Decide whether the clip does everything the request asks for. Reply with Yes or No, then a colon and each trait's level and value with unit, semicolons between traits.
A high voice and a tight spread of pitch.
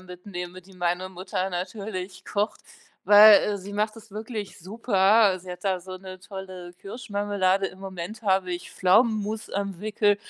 Yes: high, 195 Hz; narrow, 2.1 semitones